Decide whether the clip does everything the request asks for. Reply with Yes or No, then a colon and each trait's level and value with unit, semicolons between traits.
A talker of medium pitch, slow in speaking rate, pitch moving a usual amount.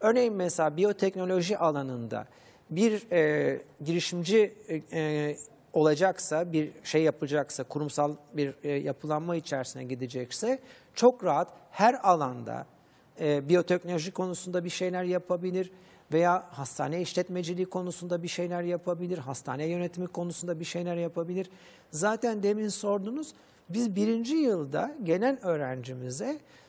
No: medium, 175 Hz; average, 110 wpm; average, 3.6 semitones